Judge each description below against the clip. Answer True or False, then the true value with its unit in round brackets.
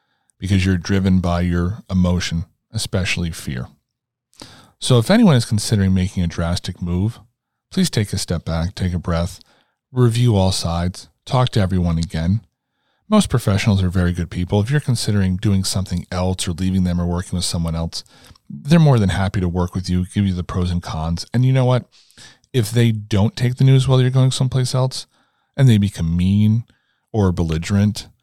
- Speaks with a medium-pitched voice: False (95 Hz)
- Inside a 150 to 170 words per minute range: False (185 wpm)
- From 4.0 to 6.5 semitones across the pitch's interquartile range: True (5.0 semitones)